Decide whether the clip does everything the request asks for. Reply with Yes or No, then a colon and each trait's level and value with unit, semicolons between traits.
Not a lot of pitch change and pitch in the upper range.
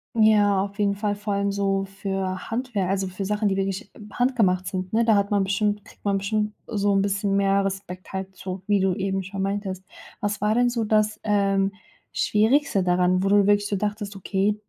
Yes: narrow, 1.4 semitones; high, 200 Hz